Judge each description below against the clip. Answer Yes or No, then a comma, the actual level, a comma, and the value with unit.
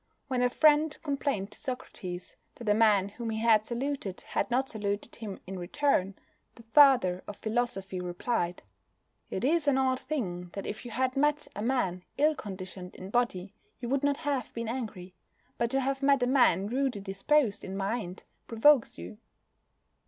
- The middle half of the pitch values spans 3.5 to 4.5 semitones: No, wide, 5.6 semitones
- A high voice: Yes, high, 230 Hz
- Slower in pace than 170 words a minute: No, average, 175 wpm